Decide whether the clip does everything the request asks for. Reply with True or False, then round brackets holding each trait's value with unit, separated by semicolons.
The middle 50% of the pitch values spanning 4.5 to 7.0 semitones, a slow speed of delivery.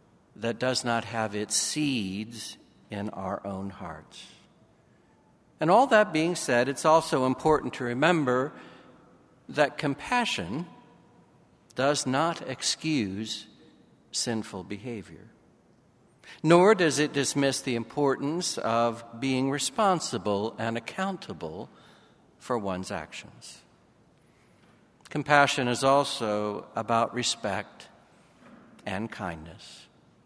True (5.2 semitones; 95 wpm)